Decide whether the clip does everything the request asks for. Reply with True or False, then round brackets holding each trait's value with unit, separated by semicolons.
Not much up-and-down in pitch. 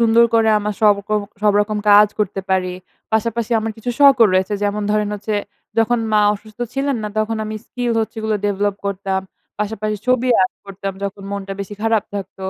True (1.9 semitones)